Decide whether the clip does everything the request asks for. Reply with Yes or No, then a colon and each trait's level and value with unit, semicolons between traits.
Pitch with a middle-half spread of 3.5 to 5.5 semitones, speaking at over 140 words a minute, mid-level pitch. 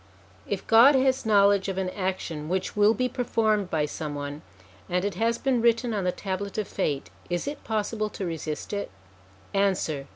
No: average, 4.0 semitones; average, 185 wpm; high, 200 Hz